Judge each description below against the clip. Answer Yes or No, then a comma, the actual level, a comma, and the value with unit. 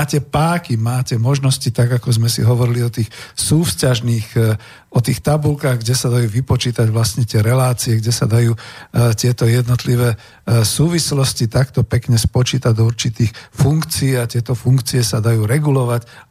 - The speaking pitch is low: Yes, low, 125 Hz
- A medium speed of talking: Yes, average, 145 wpm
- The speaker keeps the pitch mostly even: Yes, narrow, 2.1 semitones